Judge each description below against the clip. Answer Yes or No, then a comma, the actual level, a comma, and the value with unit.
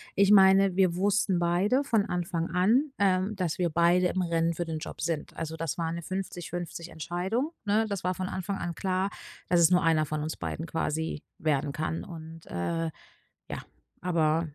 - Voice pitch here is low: No, medium, 175 Hz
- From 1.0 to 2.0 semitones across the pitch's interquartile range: No, narrow, 2.6 semitones